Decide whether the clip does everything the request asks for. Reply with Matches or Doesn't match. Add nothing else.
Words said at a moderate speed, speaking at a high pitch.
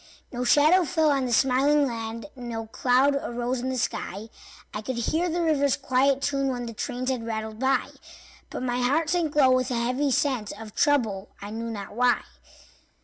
Matches